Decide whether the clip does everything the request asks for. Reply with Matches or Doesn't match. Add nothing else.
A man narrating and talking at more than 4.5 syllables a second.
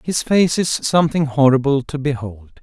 Matches